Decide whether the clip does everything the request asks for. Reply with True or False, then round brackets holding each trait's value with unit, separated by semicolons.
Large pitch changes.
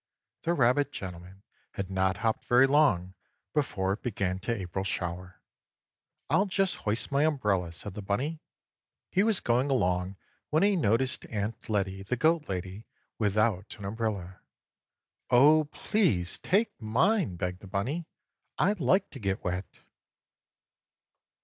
True (7.4 semitones)